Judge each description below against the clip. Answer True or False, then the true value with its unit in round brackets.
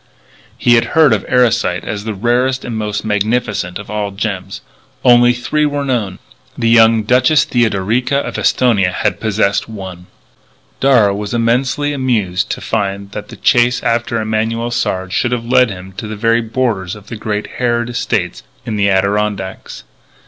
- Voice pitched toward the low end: True (110 Hz)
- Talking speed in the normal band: True (165 wpm)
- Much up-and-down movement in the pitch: False (3.1 semitones)